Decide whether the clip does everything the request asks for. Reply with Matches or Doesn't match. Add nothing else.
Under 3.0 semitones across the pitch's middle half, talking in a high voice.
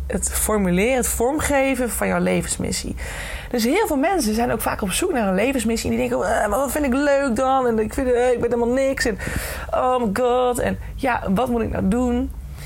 Matches